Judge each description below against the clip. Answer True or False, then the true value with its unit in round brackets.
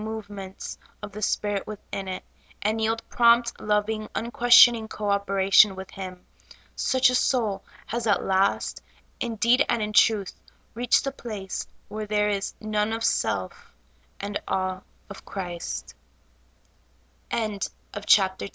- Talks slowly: True (125 wpm)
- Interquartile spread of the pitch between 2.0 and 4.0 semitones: True (2.6 semitones)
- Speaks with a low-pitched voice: False (210 Hz)